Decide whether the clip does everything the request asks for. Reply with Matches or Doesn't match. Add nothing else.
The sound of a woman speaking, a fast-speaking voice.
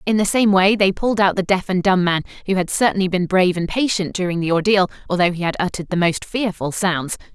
Matches